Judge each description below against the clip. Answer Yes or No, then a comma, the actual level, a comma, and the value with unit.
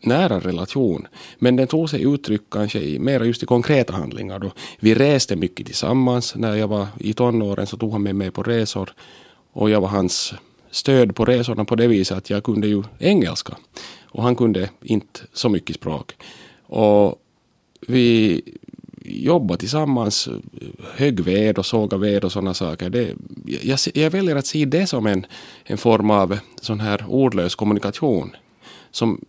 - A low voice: Yes, low, 110 Hz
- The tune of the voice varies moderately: Yes, average, 3.8 semitones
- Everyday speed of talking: No, fast, 170 wpm